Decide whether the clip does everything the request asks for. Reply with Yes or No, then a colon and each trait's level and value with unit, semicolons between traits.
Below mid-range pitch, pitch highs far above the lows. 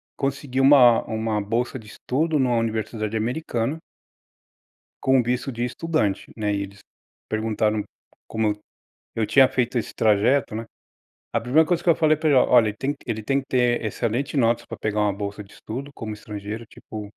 No: low, 115 Hz; average, 3.7 semitones